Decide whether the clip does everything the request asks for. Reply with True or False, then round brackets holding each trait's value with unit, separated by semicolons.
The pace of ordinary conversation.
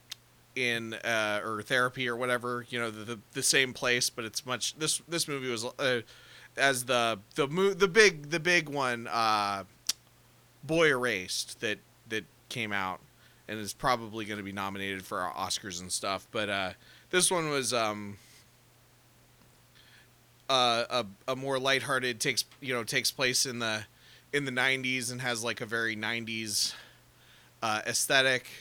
True (165 wpm)